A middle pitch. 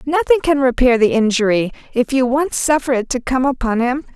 No: very high, 260 Hz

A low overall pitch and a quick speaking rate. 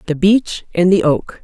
No: medium, 175 Hz; fast, 210 wpm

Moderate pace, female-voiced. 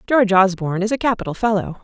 Yes: average, 195 wpm; female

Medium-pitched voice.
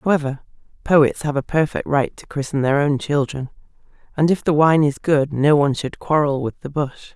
Yes: medium, 145 Hz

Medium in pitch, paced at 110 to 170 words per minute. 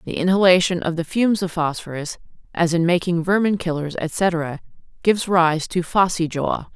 Yes: medium, 170 Hz; average, 160 wpm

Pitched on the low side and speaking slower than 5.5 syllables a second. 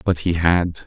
Yes: very low, 85 Hz; 3.9 syllables/s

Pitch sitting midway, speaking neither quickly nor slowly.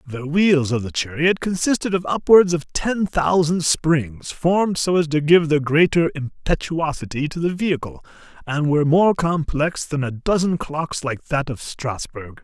Yes: medium, 155 Hz; average, 170 wpm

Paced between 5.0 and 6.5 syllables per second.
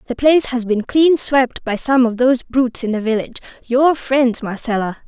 Yes: 5.3 syllables/s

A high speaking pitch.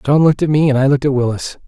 No: medium, 140 Hz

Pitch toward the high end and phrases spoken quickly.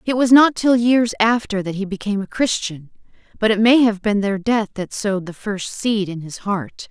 Yes: high, 210 Hz; fast, 225 wpm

